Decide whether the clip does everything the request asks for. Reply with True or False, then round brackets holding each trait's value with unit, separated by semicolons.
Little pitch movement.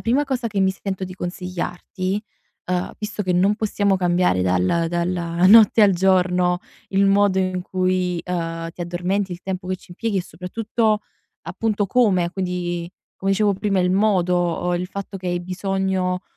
True (1.9 semitones)